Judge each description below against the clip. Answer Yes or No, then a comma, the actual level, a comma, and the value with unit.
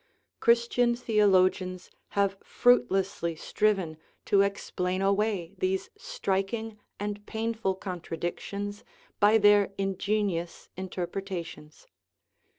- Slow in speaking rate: Yes, slow, 85 wpm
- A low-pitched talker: No, high, 195 Hz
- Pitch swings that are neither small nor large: No, narrow, 2.3 semitones